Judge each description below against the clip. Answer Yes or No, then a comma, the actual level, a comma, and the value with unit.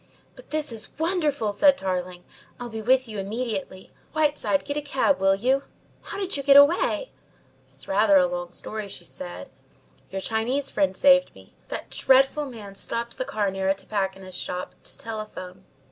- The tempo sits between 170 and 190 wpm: Yes, average, 175 wpm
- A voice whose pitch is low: No, high, 220 Hz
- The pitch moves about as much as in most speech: No, wide, 6.3 semitones